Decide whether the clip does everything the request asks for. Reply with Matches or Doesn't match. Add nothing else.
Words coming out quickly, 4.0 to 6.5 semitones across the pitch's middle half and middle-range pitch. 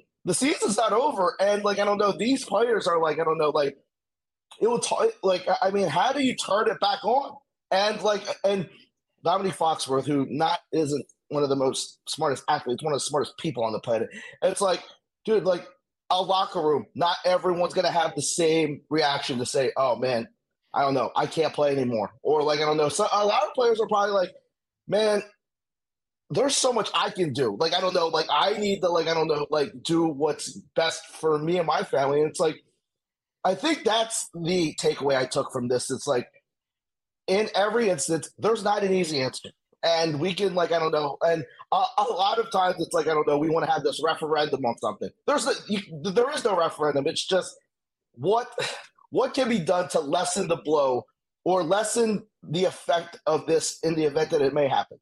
Matches